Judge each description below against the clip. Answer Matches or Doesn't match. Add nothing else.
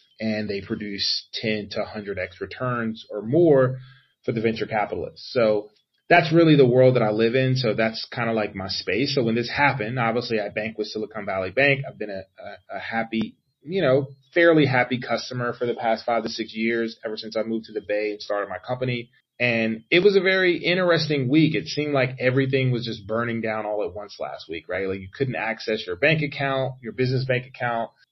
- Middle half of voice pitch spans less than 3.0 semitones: Doesn't match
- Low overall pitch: Matches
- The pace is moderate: Doesn't match